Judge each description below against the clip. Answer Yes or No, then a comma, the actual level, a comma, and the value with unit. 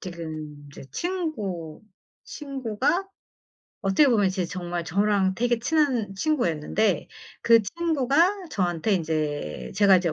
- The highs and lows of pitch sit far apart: Yes, wide, 7.9 semitones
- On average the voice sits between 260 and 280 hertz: No, high, 205 Hz